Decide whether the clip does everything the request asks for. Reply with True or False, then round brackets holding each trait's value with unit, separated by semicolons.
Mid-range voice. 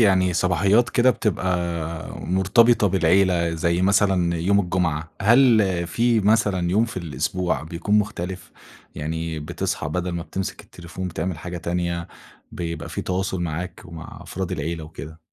False (90 Hz)